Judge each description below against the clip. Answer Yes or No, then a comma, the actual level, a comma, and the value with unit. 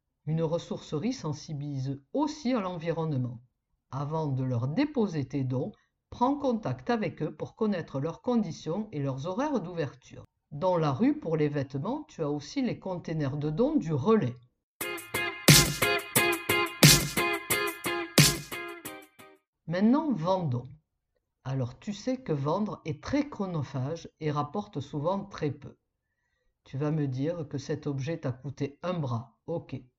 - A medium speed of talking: No, slow, 130 wpm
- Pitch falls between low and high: Yes, medium, 155 Hz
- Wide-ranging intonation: Yes, wide, 6.0 semitones